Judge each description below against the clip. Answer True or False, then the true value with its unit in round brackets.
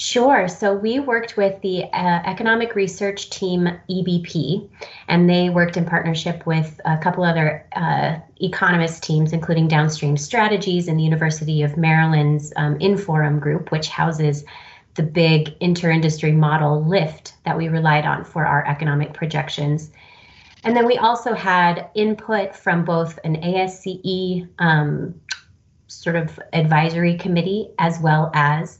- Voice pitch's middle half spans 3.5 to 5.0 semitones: False (3.1 semitones)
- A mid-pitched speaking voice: True (170 Hz)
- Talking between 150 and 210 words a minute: False (140 wpm)